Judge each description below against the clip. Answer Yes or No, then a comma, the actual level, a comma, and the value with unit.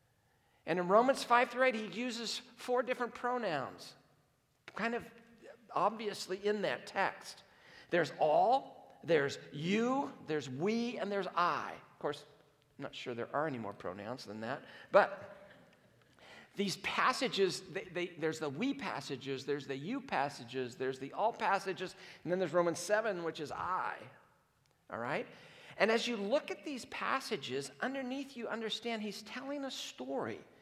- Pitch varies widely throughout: Yes, wide, 8.6 semitones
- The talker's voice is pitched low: No, high, 190 Hz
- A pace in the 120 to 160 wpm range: Yes, average, 155 wpm